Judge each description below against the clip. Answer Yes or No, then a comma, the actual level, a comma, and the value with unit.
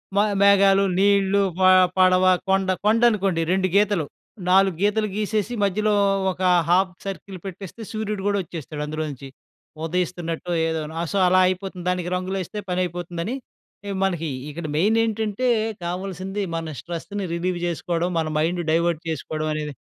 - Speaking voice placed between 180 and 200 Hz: Yes, medium, 185 Hz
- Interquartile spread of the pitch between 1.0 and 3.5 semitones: Yes, average, 2.9 semitones